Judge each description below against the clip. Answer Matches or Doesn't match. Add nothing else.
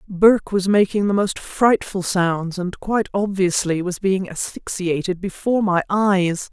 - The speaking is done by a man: Doesn't match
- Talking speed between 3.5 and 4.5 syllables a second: Matches